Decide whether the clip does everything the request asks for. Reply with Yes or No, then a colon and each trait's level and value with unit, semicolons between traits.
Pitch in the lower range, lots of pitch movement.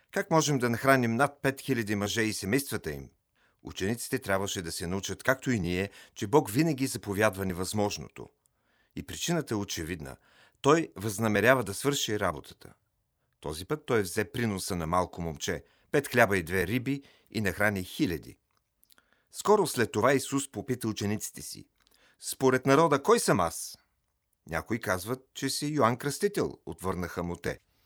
Yes: low, 110 Hz; wide, 6.0 semitones